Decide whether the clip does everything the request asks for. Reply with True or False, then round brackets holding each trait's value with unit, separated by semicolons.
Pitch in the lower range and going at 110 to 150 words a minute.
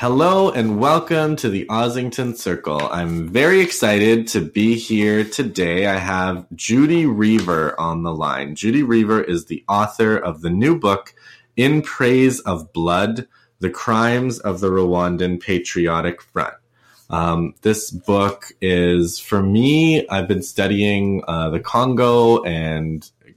True (100 Hz; 140 wpm)